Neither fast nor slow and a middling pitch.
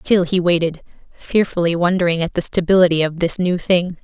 Yes: average, 180 wpm; medium, 175 Hz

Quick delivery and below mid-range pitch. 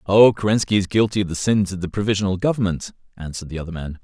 Yes: fast, 225 wpm; very low, 95 Hz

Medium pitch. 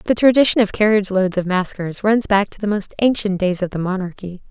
No: high, 200 Hz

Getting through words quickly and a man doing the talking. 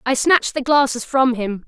No: fast, 215 wpm; female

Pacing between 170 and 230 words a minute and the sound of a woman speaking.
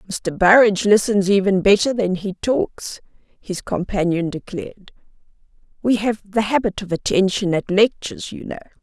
No: average, 145 wpm; female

